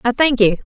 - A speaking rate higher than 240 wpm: Yes, fast, 255 wpm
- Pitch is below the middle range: No, high, 240 Hz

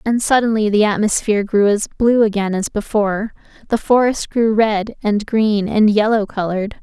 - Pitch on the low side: No, high, 210 Hz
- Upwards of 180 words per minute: No, average, 165 wpm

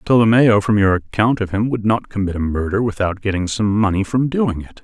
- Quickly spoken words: Yes, fast, 225 wpm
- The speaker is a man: Yes, male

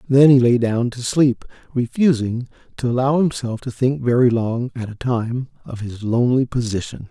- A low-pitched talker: Yes, low, 125 Hz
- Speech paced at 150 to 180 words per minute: Yes, average, 175 wpm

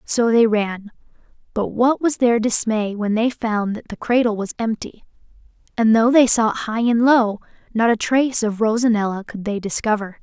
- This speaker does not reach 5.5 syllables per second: Yes, 4.8 syllables/s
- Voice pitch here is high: Yes, high, 225 Hz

